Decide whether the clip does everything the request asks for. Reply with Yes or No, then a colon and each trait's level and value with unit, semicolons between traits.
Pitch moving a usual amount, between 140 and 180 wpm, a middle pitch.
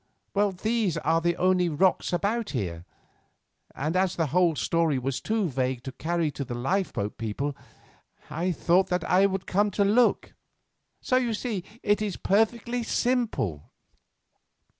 No: wide, 6.0 semitones; average, 150 wpm; medium, 180 Hz